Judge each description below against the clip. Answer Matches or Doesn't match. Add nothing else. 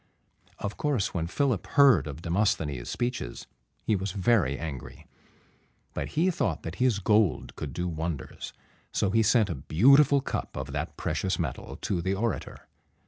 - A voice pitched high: Doesn't match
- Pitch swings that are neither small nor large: Doesn't match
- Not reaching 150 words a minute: Doesn't match